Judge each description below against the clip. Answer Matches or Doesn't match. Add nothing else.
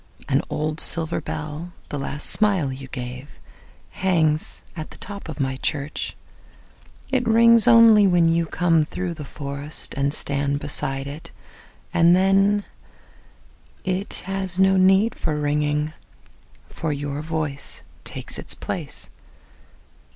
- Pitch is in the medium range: Matches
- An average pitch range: Matches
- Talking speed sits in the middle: Doesn't match